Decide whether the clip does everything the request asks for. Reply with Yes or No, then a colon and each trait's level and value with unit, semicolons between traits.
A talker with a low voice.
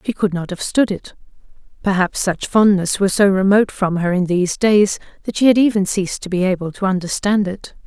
No: high, 195 Hz